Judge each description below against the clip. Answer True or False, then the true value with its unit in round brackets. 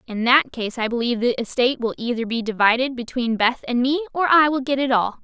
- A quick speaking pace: True (240 wpm)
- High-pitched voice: True (245 Hz)